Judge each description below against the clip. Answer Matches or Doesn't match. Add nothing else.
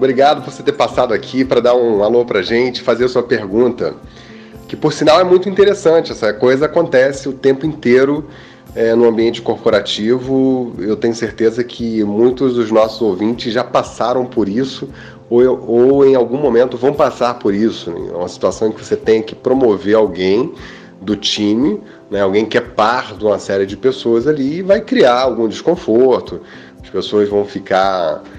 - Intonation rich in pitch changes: Doesn't match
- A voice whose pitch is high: Doesn't match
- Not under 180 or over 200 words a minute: Matches